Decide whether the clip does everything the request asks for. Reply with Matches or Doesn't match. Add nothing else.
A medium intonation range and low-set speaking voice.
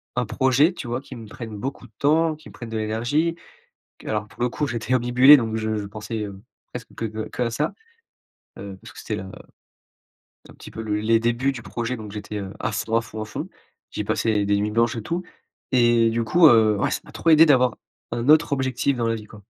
Matches